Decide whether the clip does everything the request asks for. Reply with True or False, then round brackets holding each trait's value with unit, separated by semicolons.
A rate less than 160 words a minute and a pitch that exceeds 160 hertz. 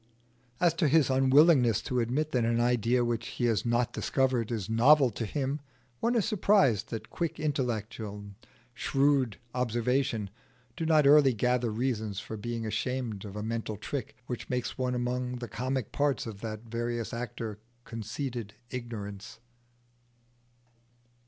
False (145 wpm; 120 Hz)